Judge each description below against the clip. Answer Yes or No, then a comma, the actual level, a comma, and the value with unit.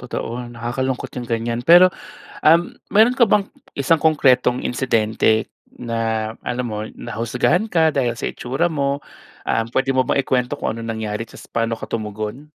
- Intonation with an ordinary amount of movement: Yes, average, 3.7 semitones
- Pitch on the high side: No, low, 125 Hz